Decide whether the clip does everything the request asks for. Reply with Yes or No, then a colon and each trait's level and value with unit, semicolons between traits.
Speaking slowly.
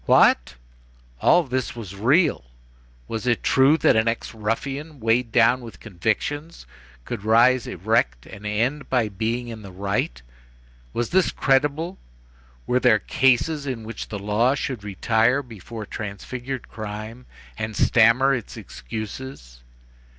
Yes: slow, 130 wpm